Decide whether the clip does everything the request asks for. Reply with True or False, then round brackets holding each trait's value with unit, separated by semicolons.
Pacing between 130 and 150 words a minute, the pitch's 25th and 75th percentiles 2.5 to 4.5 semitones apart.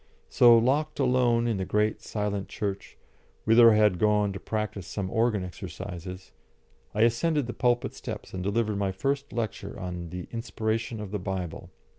False (165 wpm; 3.4 semitones)